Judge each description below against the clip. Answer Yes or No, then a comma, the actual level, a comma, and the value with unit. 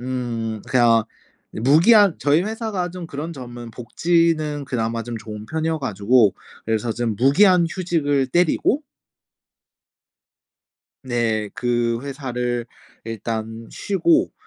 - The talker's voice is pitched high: No, low, 130 Hz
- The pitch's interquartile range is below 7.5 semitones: Yes, wide, 6.2 semitones